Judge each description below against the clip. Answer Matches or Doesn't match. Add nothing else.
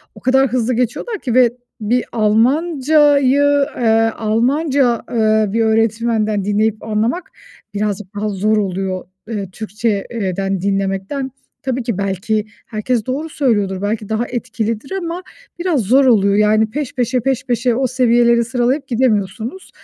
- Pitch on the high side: Matches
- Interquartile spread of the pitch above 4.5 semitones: Doesn't match